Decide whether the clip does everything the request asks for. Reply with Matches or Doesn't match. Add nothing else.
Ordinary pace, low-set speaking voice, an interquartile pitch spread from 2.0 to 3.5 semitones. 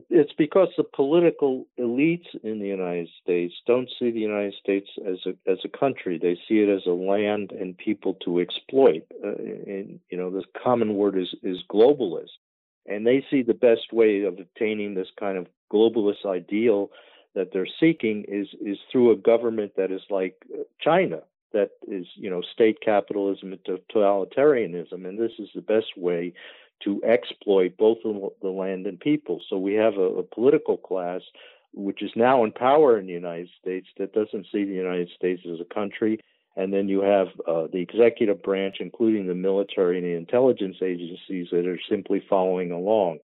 Doesn't match